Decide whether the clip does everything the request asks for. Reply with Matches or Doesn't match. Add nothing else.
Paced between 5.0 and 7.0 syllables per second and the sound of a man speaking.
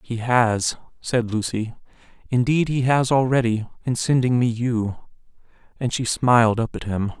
Doesn't match